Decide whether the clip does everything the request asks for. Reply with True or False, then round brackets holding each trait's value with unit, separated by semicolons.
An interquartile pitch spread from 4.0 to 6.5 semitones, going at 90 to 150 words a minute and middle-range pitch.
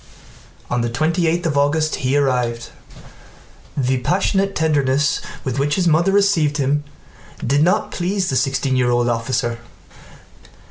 True (4.5 semitones; 140 wpm; 145 Hz)